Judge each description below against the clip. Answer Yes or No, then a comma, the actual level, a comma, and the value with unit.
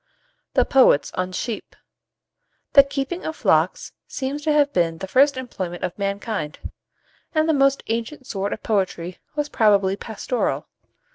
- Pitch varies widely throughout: Yes, wide, 6.5 semitones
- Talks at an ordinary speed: Yes, average, 145 wpm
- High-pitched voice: Yes, high, 230 Hz